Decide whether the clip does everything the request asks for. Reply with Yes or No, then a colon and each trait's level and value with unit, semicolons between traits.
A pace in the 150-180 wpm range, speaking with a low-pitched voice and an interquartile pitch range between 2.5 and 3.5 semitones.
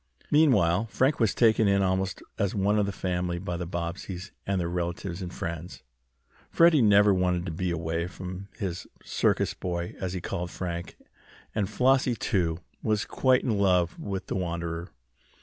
Yes: average, 165 wpm; very low, 95 Hz; average, 2.8 semitones